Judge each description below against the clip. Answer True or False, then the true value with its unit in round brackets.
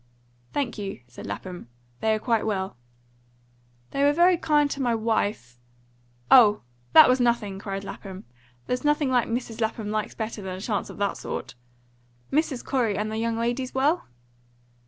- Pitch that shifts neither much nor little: True (4.3 semitones)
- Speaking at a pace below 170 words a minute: True (160 wpm)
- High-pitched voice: True (225 Hz)